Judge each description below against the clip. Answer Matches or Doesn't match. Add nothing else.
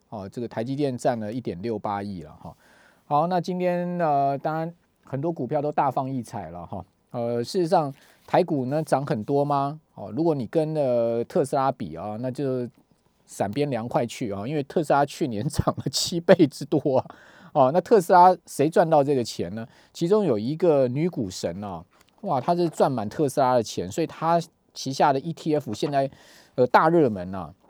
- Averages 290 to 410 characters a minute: Doesn't match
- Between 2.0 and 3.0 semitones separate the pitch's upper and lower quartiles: Doesn't match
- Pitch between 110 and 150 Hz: Matches